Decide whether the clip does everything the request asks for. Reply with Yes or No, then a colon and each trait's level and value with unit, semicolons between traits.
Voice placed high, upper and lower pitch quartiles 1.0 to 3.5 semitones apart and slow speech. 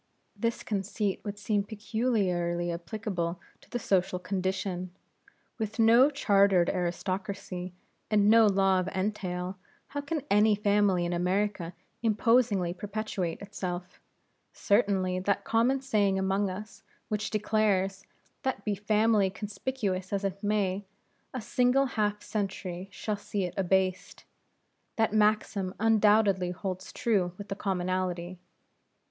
Yes: high, 200 Hz; narrow, 2.5 semitones; slow, 125 wpm